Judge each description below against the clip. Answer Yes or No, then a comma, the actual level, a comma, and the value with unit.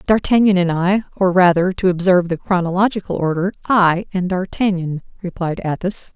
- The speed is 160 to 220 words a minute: No, average, 145 wpm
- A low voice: No, medium, 185 Hz